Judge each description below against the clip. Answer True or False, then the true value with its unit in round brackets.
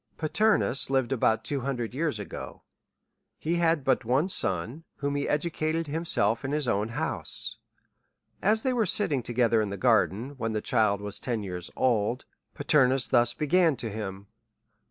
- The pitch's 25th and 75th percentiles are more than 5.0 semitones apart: True (5.5 semitones)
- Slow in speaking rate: False (165 wpm)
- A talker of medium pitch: False (130 Hz)